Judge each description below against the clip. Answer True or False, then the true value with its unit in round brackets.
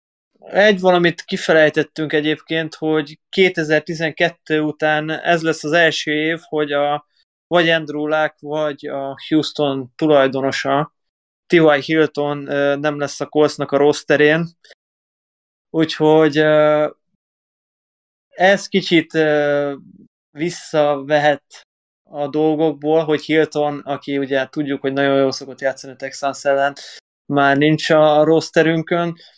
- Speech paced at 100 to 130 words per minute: True (110 wpm)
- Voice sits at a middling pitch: True (150 Hz)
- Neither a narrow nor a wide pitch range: False (2.0 semitones)